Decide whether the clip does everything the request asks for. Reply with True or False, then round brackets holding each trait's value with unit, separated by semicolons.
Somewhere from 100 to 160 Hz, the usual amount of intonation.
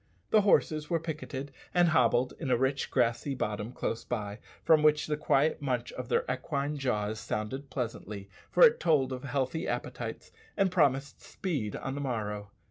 True (135 Hz; 4.2 semitones)